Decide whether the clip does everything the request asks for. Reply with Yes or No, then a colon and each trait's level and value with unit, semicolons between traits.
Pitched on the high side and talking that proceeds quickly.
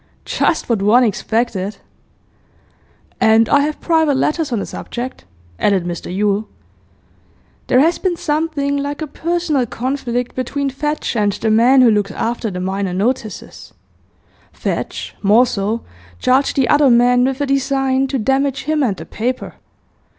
No: very high, 250 Hz; average, 150 wpm